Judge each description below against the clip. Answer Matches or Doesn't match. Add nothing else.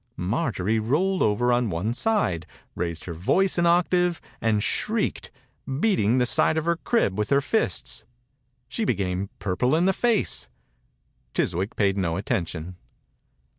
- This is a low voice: Matches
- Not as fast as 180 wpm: Matches